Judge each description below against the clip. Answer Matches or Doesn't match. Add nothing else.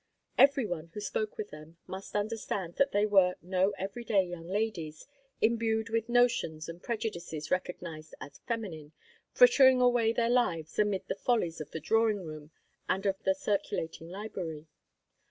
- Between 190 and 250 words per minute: Doesn't match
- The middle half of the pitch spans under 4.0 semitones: Doesn't match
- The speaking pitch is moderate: Doesn't match